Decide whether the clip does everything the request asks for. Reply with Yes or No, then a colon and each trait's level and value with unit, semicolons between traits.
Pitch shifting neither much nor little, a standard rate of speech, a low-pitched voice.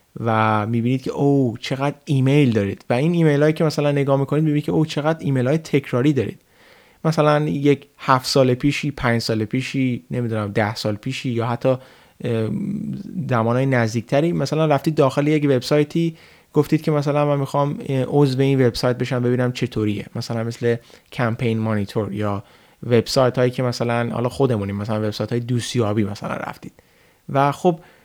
No: average, 3.8 semitones; fast, 160 wpm; low, 130 Hz